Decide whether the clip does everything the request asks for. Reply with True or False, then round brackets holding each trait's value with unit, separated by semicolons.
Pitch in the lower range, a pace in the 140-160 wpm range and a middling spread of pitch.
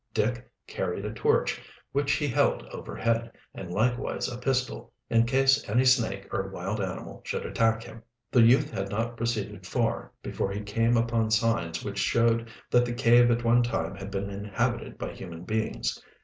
False (115 Hz; 175 wpm; 3.0 semitones)